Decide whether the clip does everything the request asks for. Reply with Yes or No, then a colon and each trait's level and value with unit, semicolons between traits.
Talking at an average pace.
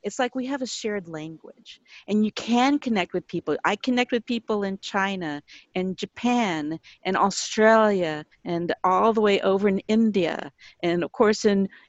Yes: average, 170 wpm